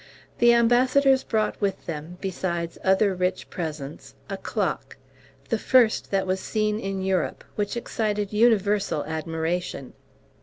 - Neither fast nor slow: No, slow, 125 wpm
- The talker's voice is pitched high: Yes, high, 195 Hz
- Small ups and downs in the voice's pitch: No, average, 3.9 semitones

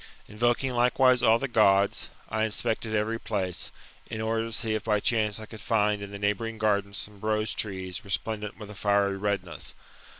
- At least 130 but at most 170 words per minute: No, average, 180 wpm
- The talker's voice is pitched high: No, low, 105 Hz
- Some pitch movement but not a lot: No, narrow, 1.8 semitones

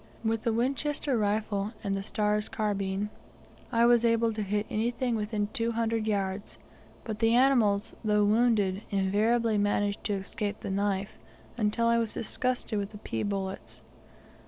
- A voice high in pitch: Yes, high, 215 Hz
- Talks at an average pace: Yes, average, 155 wpm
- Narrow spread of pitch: Yes, narrow, 2.2 semitones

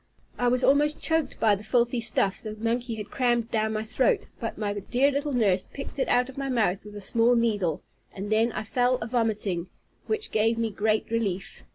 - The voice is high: Yes, high, 230 Hz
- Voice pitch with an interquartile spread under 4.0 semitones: Yes, average, 2.8 semitones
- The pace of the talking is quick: Yes, fast, 210 wpm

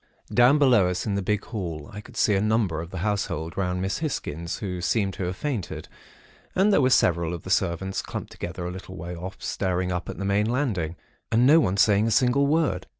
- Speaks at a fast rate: Yes, fast, 225 wpm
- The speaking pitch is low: Yes, very low, 95 Hz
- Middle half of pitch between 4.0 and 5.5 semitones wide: Yes, average, 4.3 semitones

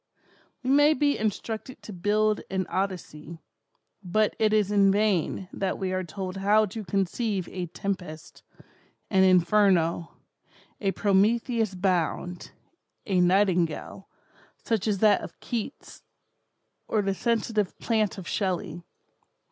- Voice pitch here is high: Yes, high, 195 Hz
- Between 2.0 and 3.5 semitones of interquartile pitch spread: Yes, average, 2.8 semitones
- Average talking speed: No, slow, 125 wpm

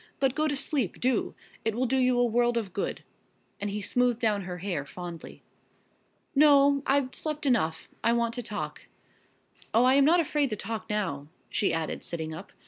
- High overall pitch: Yes, high, 235 Hz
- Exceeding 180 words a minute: Yes, average, 190 wpm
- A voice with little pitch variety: No, average, 5.2 semitones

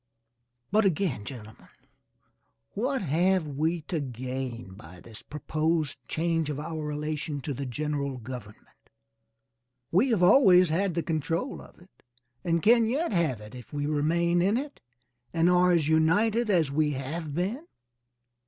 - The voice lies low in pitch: No, medium, 160 Hz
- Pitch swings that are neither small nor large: Yes, average, 4.3 semitones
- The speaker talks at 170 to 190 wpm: No, average, 145 wpm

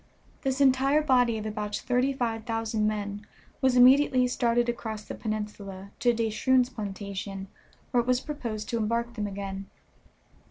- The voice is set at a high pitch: Yes, high, 230 Hz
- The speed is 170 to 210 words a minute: No, average, 155 wpm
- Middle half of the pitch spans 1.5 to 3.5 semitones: Yes, average, 3.2 semitones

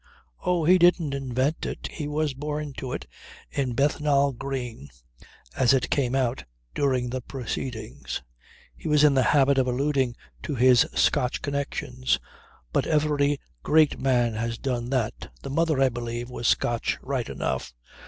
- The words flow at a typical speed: Yes, average, 155 wpm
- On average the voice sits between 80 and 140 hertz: Yes, low, 135 Hz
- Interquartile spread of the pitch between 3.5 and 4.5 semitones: No, average, 2.9 semitones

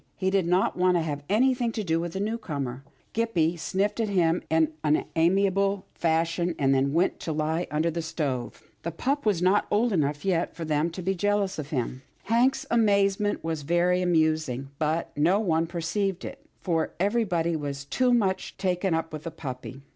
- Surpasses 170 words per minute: Yes, average, 185 wpm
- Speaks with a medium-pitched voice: Yes, medium, 170 Hz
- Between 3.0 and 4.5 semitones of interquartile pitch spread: Yes, average, 3.9 semitones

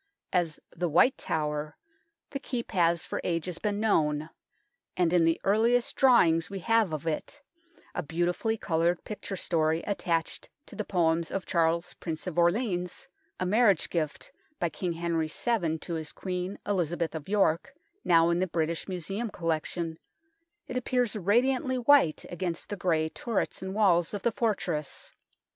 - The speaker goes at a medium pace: Yes, average, 160 wpm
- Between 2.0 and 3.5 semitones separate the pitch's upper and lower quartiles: No, average, 4.2 semitones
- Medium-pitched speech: Yes, medium, 175 Hz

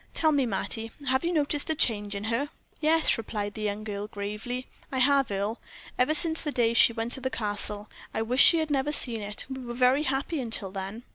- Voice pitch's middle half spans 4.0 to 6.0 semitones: Yes, average, 5.0 semitones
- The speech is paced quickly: Yes, fast, 220 wpm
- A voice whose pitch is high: Yes, high, 240 Hz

